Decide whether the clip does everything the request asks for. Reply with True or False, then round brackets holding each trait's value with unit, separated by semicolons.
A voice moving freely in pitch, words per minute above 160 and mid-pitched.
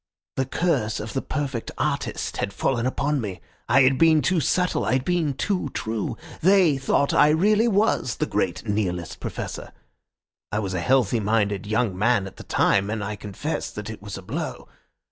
False (6.3 semitones; 185 wpm; 120 Hz)